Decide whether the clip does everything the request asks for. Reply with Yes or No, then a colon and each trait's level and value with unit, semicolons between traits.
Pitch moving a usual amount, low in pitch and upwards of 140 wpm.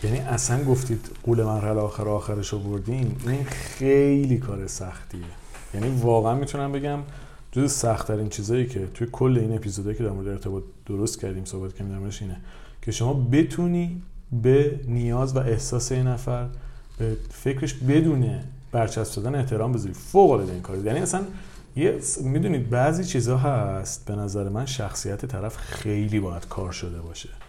Yes: average, 4.1 semitones; low, 120 Hz; fast, 155 wpm